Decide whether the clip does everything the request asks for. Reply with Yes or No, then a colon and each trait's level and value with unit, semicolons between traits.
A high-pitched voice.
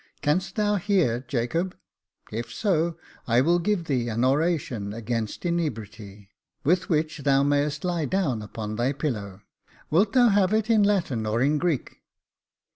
No: medium, 145 Hz